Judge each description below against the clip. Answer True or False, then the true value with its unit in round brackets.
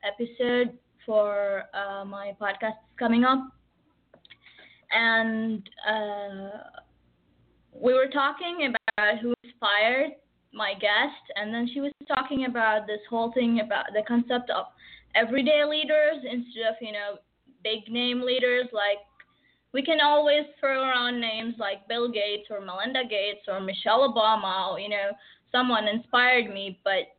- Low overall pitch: False (225 Hz)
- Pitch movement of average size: True (3.6 semitones)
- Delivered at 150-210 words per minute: False (135 wpm)